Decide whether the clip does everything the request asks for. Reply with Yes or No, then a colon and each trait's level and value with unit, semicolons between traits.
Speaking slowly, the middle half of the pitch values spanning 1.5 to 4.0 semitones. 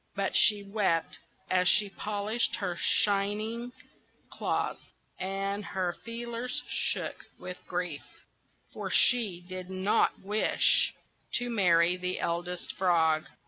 Yes: slow, 110 wpm; average, 2.9 semitones